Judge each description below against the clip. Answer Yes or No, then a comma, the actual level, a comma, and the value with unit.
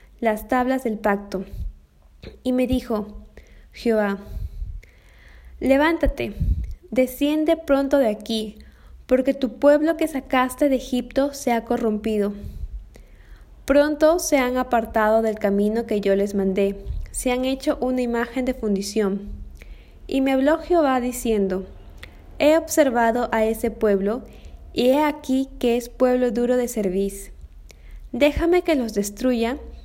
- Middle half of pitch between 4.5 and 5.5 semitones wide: Yes, average, 4.8 semitones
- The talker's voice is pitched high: Yes, high, 235 Hz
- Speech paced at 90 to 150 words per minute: Yes, slow, 125 wpm